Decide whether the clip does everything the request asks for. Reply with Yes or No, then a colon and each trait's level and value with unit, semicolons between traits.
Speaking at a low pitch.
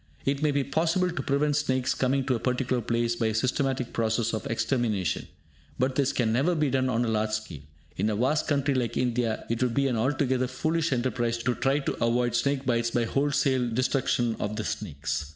Yes: low, 125 Hz